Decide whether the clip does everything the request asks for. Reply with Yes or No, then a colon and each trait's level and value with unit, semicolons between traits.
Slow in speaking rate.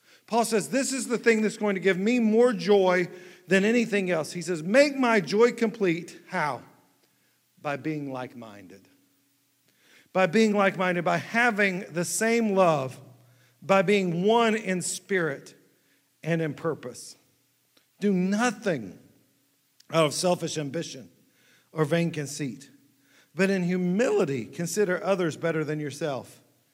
Yes: slow, 130 wpm